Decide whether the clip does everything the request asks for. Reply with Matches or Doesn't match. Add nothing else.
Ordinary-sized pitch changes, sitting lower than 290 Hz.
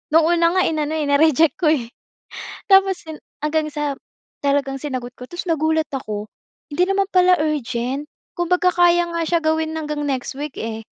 Doesn't match